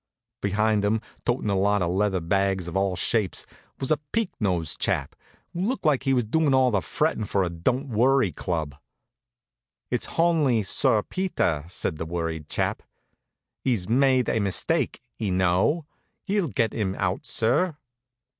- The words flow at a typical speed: Yes, average, 160 wpm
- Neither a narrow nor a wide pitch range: No, wide, 6.5 semitones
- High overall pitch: No, low, 105 Hz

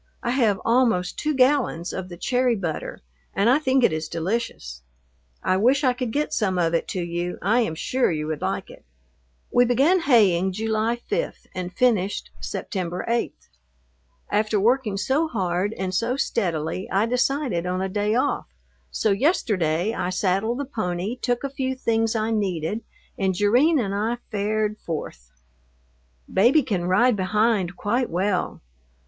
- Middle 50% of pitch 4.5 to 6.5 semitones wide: Yes, average, 5.2 semitones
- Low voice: No, high, 210 Hz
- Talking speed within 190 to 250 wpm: No, average, 160 wpm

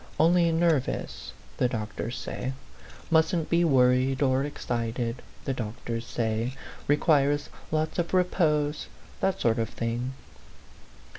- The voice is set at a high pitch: No, low, 135 Hz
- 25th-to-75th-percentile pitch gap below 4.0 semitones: No, average, 5.1 semitones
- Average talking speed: No, slow, 125 wpm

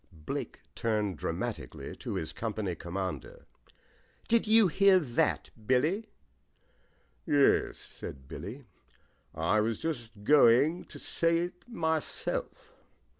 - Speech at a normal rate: No, slow, 115 wpm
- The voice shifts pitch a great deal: Yes, wide, 8.4 semitones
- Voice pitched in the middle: No, low, 125 Hz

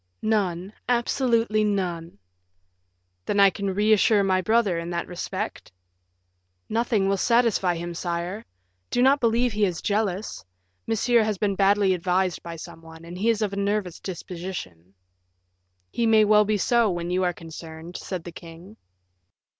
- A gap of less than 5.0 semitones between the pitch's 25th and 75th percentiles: Yes, average, 3.7 semitones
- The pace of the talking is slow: No, average, 150 wpm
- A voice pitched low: No, high, 195 Hz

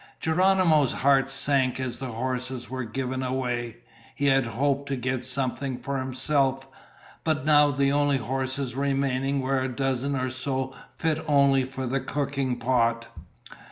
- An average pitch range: No, narrow, 1.4 semitones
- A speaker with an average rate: Yes, average, 150 wpm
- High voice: No, low, 135 Hz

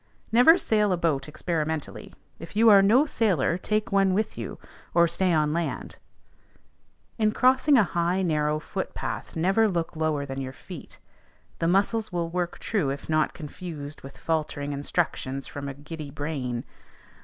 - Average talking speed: Yes, average, 160 wpm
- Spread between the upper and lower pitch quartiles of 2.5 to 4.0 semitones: No, average, 4.8 semitones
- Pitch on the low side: No, medium, 165 Hz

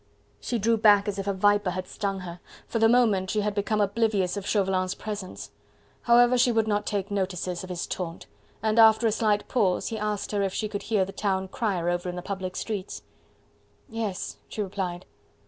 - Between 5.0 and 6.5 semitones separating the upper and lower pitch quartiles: No, narrow, 2.6 semitones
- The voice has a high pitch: Yes, high, 205 Hz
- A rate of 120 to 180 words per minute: No, average, 200 wpm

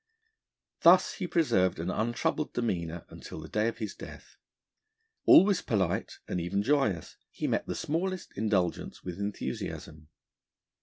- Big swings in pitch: Yes, wide, 9.0 semitones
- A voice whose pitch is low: Yes, low, 105 Hz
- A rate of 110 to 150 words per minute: Yes, slow, 135 wpm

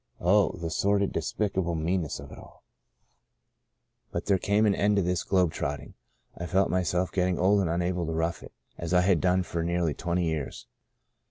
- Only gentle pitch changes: Yes, narrow, 2.3 semitones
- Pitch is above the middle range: No, very low, 90 Hz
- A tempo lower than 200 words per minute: No, fast, 205 wpm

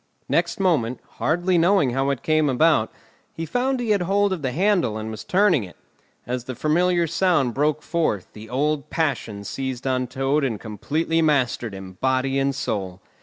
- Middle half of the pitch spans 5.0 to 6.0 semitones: Yes, wide, 5.6 semitones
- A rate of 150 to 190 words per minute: Yes, average, 175 wpm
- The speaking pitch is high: No, medium, 140 Hz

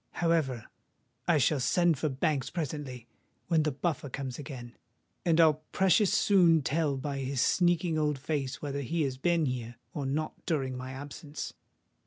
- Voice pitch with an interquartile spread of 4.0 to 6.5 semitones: No, average, 3.6 semitones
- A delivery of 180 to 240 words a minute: No, average, 160 wpm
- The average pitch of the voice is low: No, medium, 145 Hz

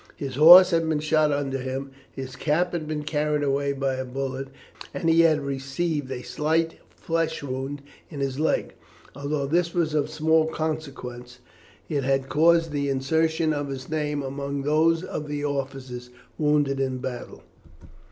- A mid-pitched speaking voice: Yes, medium, 145 Hz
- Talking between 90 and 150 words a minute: No, average, 165 wpm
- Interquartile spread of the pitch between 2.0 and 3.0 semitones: Yes, average, 2.7 semitones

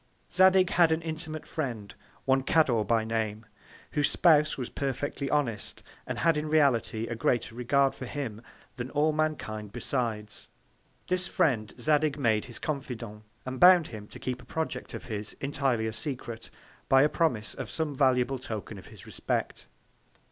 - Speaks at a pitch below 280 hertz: Yes, low, 135 Hz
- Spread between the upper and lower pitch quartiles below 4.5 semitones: No, average, 5.2 semitones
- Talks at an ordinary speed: Yes, average, 160 wpm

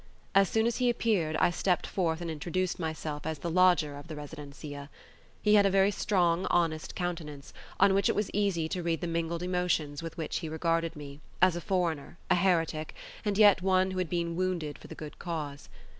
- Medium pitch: Yes, medium, 170 Hz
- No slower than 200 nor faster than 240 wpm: Yes, fast, 205 wpm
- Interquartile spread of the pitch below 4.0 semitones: Yes, average, 2.8 semitones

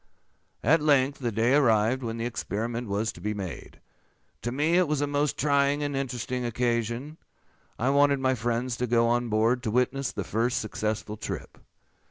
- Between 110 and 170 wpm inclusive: No, average, 180 wpm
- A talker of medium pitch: No, low, 125 Hz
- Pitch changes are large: No, average, 3.4 semitones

